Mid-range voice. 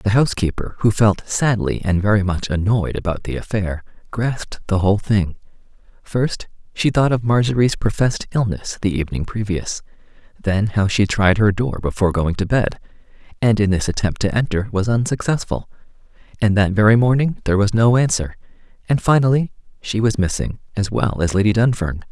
No: low, 105 Hz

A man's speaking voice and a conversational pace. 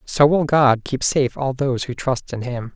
No: male; fast, 240 wpm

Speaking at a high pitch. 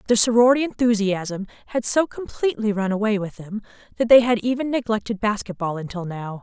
Yes: high, 215 Hz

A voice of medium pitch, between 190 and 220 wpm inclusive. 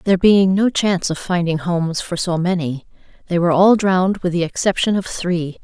Yes: medium, 180 Hz; average, 200 wpm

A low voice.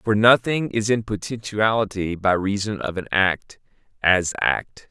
Yes: low, 105 Hz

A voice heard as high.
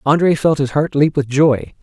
No: medium, 145 Hz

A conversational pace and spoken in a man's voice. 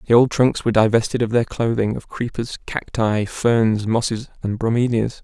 Yes: average, 170 wpm; male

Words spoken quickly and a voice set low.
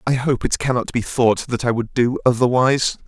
Yes: fast, 215 wpm; low, 125 Hz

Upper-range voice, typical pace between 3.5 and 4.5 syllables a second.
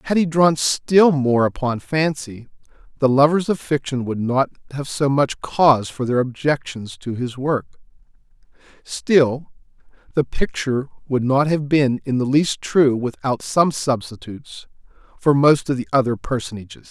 No: low, 135 Hz; 4.4 syllables/s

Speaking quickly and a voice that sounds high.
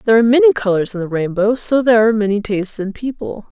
Yes: fast, 235 wpm; high, 210 Hz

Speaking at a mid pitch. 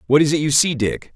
Yes: medium, 145 Hz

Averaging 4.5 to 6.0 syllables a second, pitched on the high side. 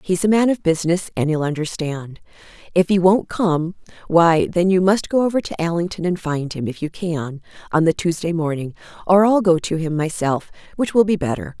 No: 5.3 syllables/s; medium, 170 Hz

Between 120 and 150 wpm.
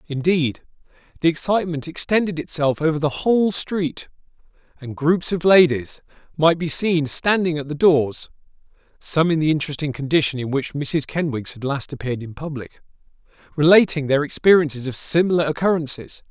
Yes: average, 145 wpm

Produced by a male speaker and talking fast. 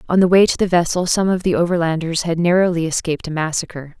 No: female; fast, 225 wpm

